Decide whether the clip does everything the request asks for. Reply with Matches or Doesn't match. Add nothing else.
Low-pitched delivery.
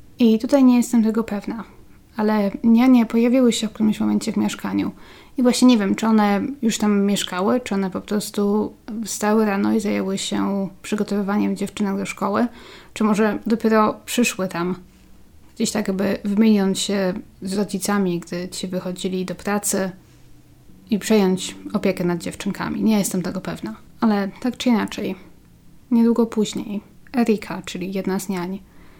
Doesn't match